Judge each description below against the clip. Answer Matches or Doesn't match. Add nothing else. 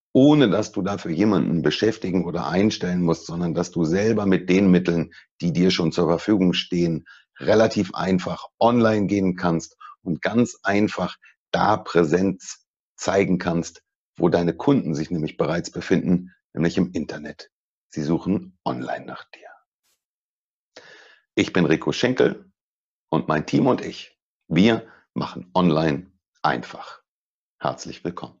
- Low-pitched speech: Matches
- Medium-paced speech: Matches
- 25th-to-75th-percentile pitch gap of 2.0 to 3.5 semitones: Matches